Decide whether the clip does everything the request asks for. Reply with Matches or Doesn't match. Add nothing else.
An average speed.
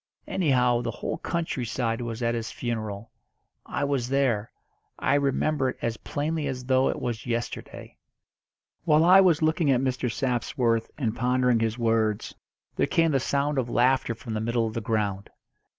Matches